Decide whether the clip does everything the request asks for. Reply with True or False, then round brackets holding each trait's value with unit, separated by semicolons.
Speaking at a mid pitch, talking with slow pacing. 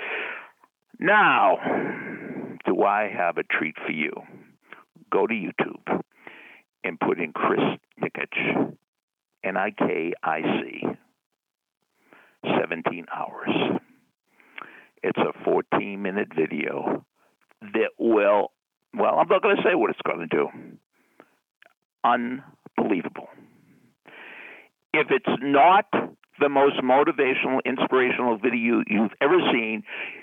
False (120 Hz; 105 wpm)